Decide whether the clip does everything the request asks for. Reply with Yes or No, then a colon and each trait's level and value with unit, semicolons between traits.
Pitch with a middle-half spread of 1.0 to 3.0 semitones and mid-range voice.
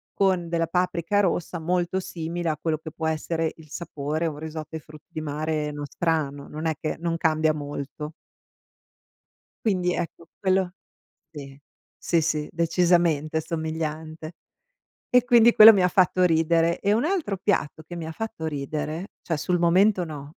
Yes: narrow, 2.4 semitones; medium, 165 Hz